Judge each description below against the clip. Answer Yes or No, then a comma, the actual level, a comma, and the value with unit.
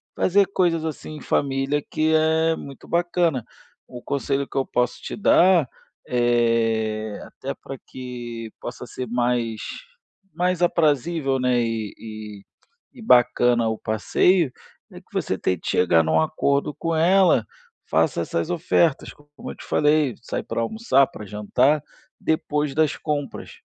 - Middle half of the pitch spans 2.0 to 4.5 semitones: No, wide, 5.4 semitones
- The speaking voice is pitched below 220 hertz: Yes, low, 135 Hz